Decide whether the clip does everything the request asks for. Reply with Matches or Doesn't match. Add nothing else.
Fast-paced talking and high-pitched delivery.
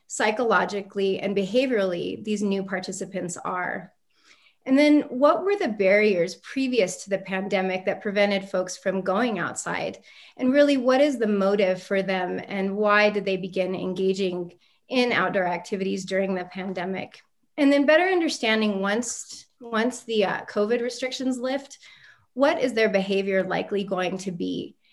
Doesn't match